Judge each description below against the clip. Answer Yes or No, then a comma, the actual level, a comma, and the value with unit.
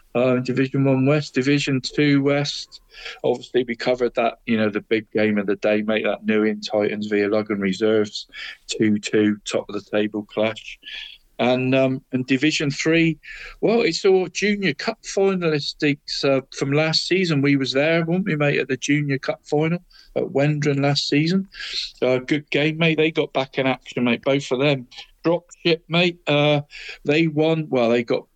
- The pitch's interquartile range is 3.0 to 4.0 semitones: No, average, 4.6 semitones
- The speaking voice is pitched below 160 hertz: Yes, medium, 140 Hz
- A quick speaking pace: No, average, 180 wpm